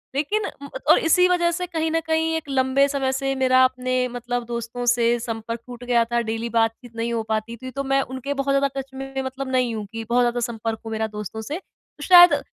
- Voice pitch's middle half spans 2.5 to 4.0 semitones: Yes, average, 2.9 semitones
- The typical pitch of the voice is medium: No, very high, 255 Hz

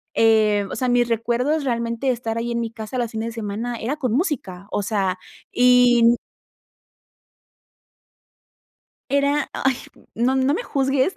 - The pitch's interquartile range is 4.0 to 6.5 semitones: No, average, 2.8 semitones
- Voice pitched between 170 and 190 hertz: No, high, 240 Hz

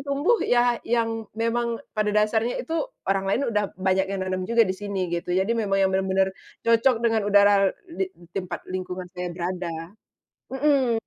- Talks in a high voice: Yes, high, 205 Hz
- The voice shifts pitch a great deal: No, average, 3.7 semitones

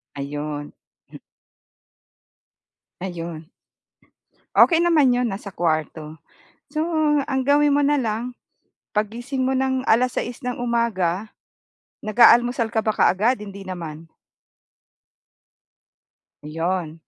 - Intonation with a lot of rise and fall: Yes, wide, 6.9 semitones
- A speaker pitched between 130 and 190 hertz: No, high, 220 Hz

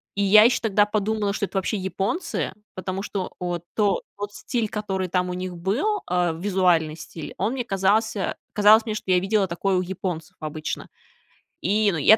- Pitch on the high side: Yes, high, 195 Hz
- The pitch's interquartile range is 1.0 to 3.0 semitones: Yes, average, 2.7 semitones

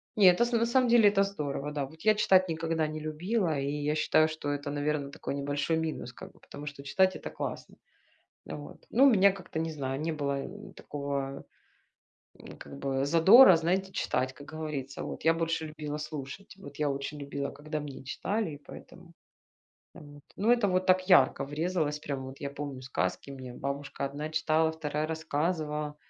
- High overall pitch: No, medium, 150 Hz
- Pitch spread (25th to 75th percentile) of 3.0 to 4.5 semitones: Yes, average, 3.7 semitones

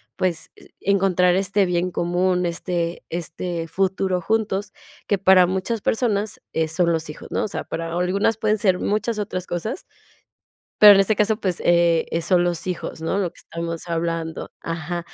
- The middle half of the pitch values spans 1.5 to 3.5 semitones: Yes, average, 2.8 semitones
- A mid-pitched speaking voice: Yes, medium, 180 Hz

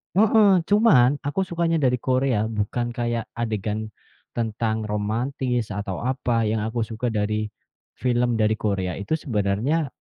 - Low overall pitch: Yes, low, 115 Hz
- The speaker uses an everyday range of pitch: Yes, average, 3.1 semitones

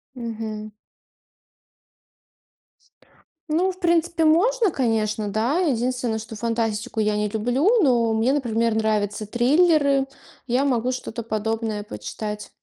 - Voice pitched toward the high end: Yes, high, 235 Hz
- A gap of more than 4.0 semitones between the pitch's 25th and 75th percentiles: Yes, average, 4.6 semitones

